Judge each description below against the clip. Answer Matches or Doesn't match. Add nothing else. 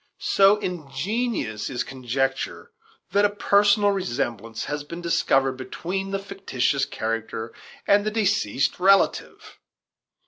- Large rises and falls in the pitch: Matches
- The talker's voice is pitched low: Doesn't match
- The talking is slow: Matches